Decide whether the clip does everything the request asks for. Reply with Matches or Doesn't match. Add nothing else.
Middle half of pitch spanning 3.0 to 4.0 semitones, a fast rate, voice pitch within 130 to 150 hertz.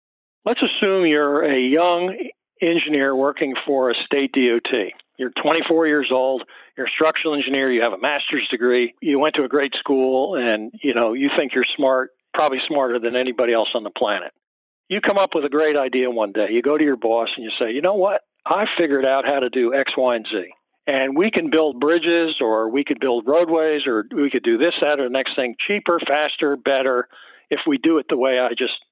Matches